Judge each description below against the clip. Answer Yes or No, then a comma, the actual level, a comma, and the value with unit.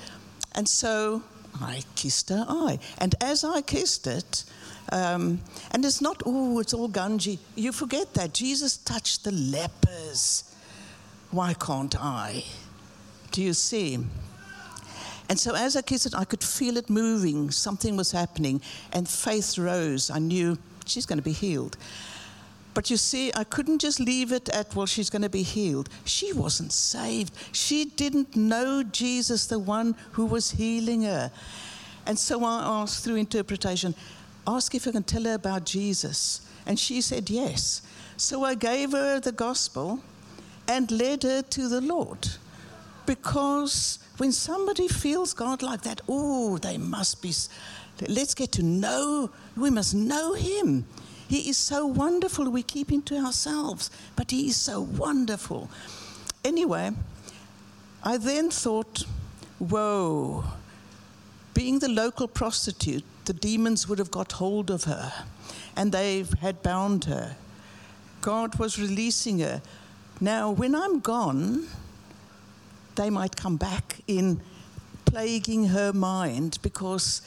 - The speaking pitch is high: Yes, high, 215 Hz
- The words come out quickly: No, average, 145 wpm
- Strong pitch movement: Yes, wide, 6.9 semitones